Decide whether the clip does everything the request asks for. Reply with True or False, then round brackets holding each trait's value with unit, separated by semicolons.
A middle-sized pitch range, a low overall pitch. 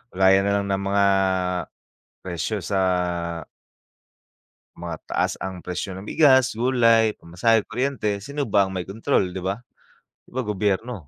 True (3.5 semitones; 100 Hz)